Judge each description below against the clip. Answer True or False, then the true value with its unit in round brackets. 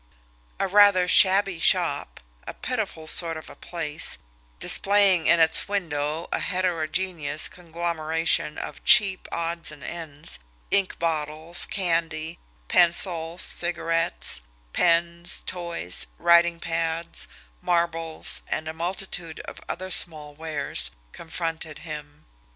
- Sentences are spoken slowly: True (110 wpm)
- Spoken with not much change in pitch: True (1.9 semitones)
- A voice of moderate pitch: True (165 Hz)